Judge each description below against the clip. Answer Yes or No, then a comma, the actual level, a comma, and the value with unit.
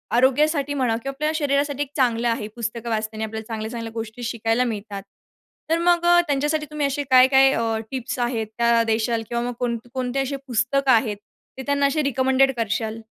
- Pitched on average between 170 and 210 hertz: No, high, 245 Hz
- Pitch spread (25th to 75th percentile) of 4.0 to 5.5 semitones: No, average, 3.5 semitones